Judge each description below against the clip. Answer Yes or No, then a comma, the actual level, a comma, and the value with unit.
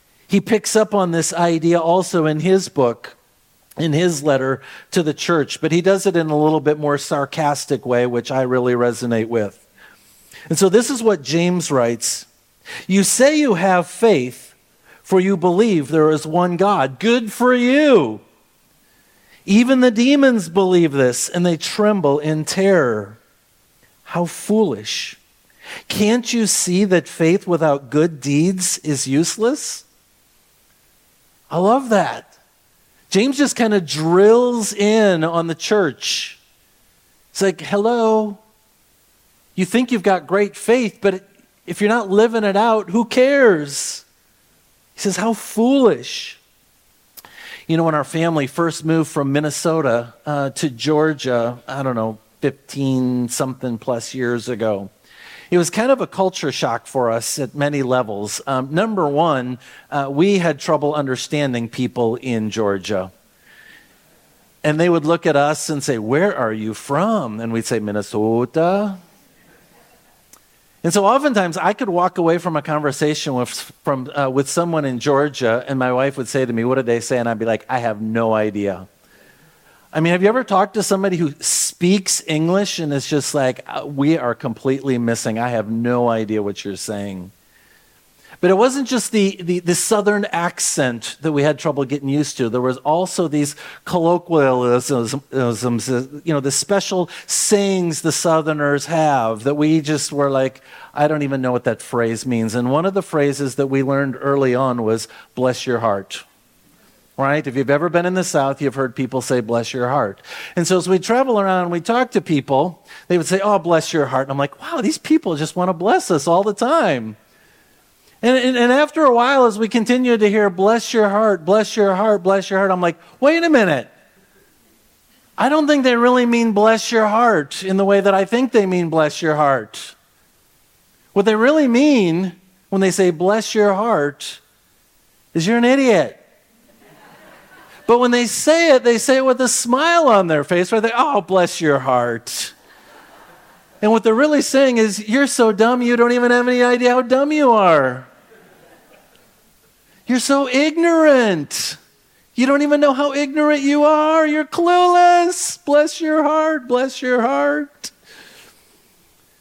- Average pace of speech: Yes, average, 170 wpm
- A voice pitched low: No, medium, 170 Hz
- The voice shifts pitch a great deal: Yes, wide, 7.8 semitones